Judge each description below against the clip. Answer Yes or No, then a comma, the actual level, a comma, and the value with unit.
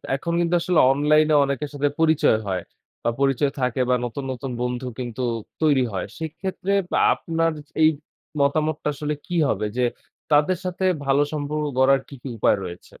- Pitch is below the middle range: No, medium, 145 Hz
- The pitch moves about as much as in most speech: Yes, average, 3.4 semitones